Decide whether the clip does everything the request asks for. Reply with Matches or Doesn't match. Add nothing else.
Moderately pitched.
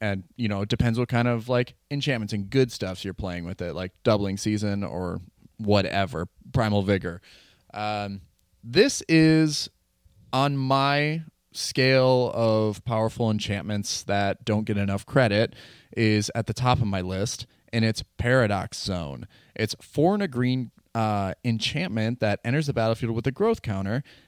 Doesn't match